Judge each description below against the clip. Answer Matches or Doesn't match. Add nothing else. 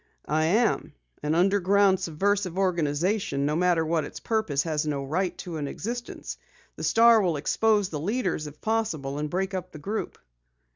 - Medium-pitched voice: Matches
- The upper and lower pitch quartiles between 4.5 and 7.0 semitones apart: Matches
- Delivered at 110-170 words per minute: Matches